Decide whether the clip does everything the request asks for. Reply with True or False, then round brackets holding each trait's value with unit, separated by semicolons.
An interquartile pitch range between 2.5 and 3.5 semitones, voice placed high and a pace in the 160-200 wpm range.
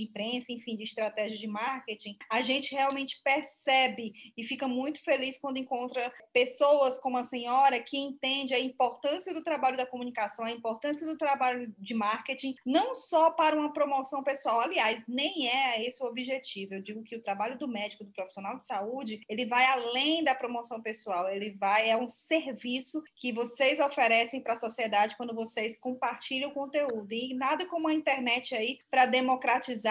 True (3.2 semitones; 250 Hz; 175 wpm)